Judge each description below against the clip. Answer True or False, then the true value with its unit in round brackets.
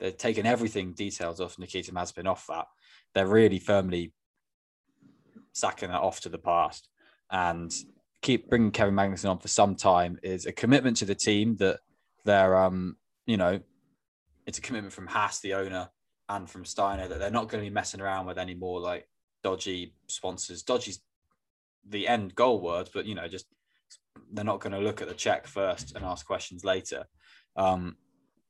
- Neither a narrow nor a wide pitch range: False (2.0 semitones)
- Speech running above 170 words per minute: True (180 wpm)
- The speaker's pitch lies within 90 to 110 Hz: True (95 Hz)